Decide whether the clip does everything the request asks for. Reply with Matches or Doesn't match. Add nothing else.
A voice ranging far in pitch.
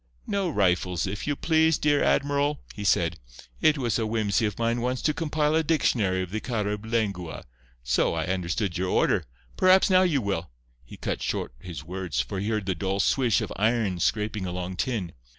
Matches